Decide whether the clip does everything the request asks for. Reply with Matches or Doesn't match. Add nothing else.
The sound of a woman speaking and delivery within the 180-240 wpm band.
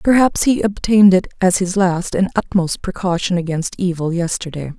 Doesn't match